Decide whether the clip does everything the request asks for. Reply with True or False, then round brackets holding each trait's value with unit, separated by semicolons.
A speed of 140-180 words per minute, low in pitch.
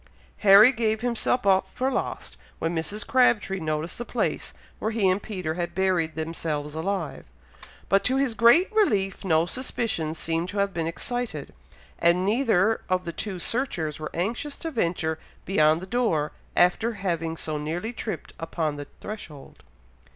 False (160 wpm; 190 Hz)